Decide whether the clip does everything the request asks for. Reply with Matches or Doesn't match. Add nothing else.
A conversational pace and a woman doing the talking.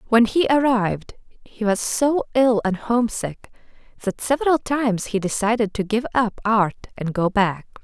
Matches